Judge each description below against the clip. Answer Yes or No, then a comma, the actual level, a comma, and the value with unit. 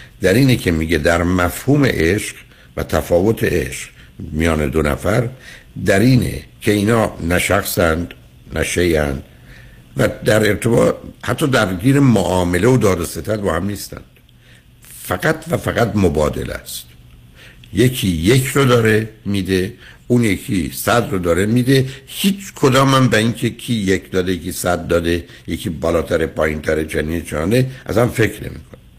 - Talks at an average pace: Yes, average, 145 wpm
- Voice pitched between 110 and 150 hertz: No, low, 100 Hz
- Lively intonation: Yes, wide, 6.2 semitones